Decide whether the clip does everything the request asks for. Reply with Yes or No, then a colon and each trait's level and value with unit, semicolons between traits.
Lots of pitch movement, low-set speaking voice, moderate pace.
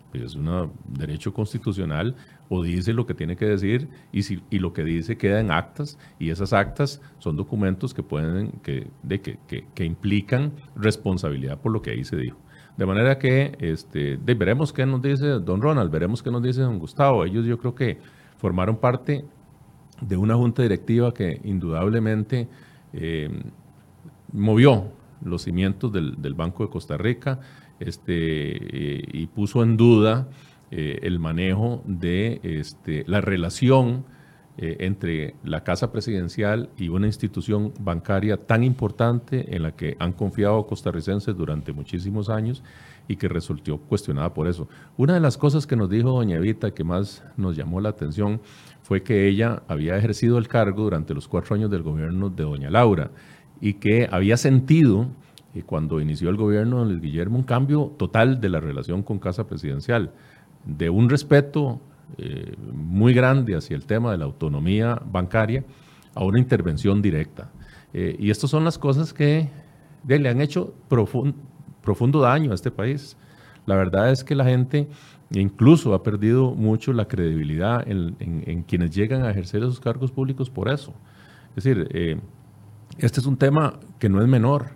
Yes: wide, 6.1 semitones; low, 110 Hz; average, 170 wpm